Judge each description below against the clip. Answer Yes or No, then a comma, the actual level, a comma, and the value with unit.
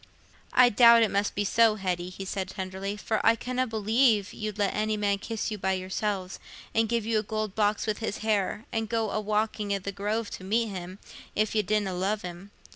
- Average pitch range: No, narrow, 2.1 semitones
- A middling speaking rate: No, fast, 215 wpm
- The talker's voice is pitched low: No, high, 210 Hz